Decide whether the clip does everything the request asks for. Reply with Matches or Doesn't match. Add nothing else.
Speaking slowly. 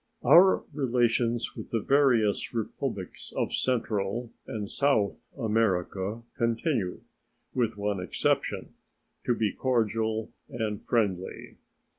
Matches